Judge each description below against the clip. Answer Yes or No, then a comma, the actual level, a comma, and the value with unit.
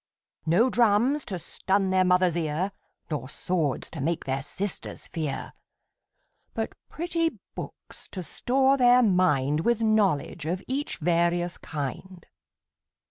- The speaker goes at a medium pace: No, slow, 125 wpm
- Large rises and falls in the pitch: Yes, wide, 6.0 semitones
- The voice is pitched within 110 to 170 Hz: No, medium, 180 Hz